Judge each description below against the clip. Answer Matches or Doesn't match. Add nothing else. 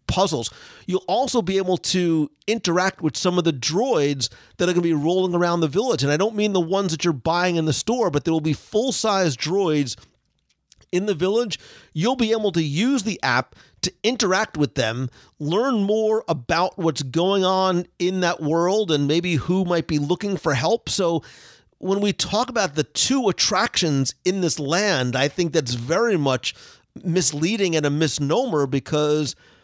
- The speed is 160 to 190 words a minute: Matches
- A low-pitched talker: Doesn't match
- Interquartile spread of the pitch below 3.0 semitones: Doesn't match